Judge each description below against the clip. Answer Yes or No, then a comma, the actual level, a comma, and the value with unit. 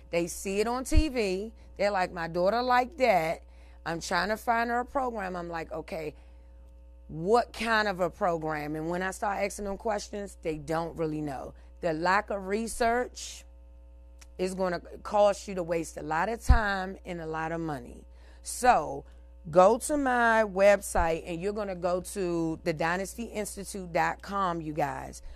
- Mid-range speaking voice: Yes, medium, 180 Hz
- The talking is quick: No, average, 170 wpm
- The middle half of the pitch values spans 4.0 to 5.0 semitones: Yes, average, 4.7 semitones